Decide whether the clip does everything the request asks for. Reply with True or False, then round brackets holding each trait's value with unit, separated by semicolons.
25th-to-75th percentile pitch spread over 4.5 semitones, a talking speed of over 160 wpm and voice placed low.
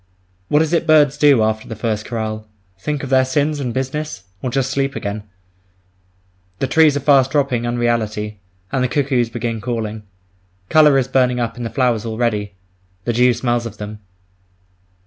False (3.6 semitones; 170 wpm; 125 Hz)